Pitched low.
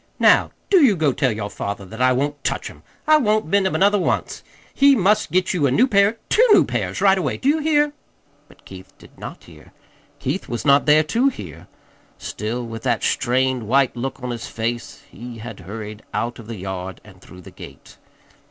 Yes: low, 130 Hz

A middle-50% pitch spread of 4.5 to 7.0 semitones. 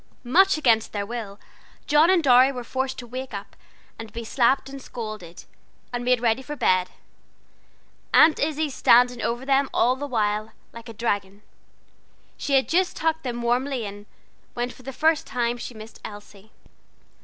No: average, 3.6 semitones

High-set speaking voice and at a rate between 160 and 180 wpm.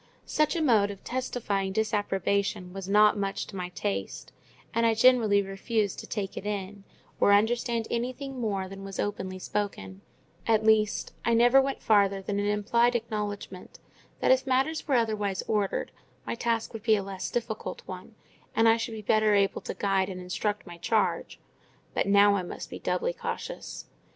Yes: high, 210 Hz; average, 175 wpm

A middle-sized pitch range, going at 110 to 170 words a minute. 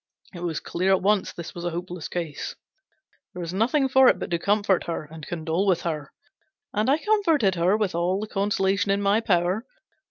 No: average, 3.4 semitones; average, 200 wpm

